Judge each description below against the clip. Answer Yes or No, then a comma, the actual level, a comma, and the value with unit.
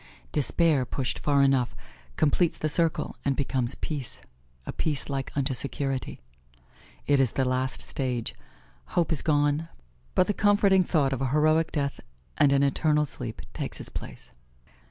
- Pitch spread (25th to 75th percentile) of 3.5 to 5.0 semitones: No, narrow, 2.6 semitones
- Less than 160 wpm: Yes, average, 150 wpm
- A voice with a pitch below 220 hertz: Yes, medium, 140 Hz